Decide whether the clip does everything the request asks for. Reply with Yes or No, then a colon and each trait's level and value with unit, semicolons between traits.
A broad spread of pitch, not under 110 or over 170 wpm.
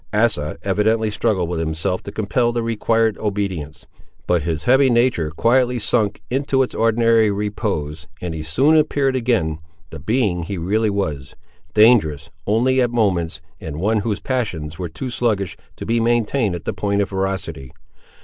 Yes: wide, 5.9 semitones; average, 165 wpm